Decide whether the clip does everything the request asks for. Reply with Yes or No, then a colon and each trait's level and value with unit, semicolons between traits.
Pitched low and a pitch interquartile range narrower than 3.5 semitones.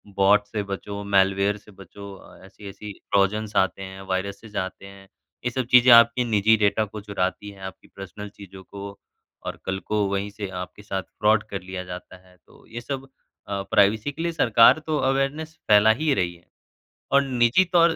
Yes: low, 100 Hz; average, 2.8 semitones